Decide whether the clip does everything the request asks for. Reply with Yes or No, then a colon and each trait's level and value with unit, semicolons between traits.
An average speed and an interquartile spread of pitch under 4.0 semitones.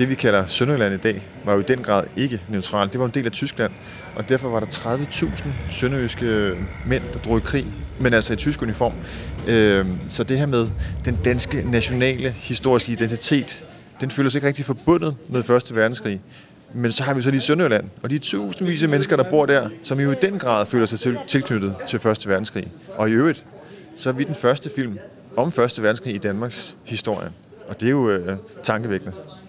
No: average, 205 wpm; average, 4.3 semitones